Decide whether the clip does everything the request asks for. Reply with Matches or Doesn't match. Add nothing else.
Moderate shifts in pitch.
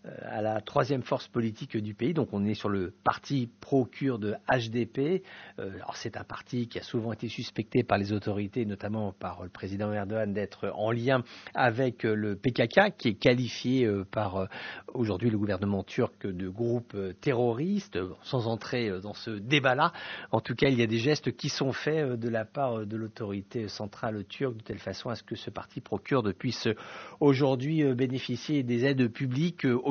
Matches